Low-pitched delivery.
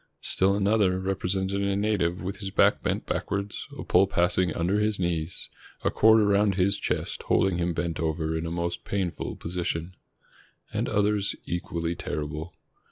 Yes: very low, 95 Hz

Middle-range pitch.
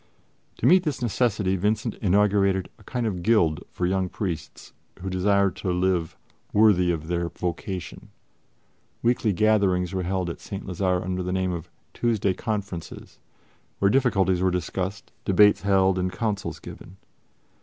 No: very low, 95 Hz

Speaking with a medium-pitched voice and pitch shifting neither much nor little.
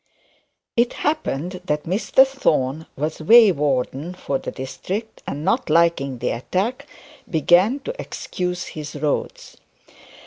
No: medium, 170 Hz; wide, 7.1 semitones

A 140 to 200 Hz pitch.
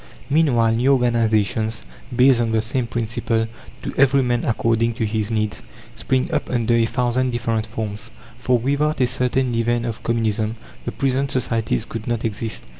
No: low, 115 Hz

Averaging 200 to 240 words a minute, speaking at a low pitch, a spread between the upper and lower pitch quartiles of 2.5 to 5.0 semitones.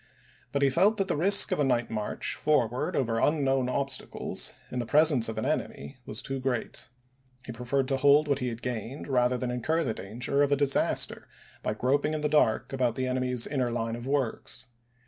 Yes: fast, 205 wpm; low, 130 Hz; average, 3.0 semitones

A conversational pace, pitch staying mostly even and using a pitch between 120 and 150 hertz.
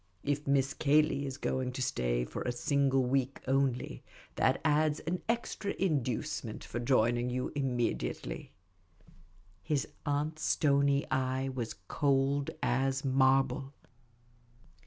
No: slow, 115 wpm; narrow, 2.0 semitones; low, 135 Hz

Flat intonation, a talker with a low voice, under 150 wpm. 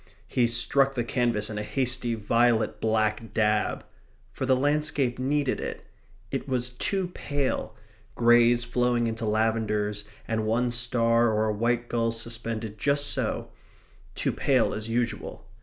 Yes: narrow, 2.0 semitones; low, 120 Hz; average, 140 wpm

